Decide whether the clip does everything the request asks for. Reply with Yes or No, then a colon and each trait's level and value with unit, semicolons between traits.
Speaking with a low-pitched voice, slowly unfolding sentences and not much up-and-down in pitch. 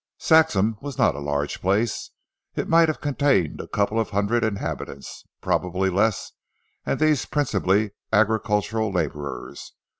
No: low, 105 Hz; slow, 130 wpm; average, 4.2 semitones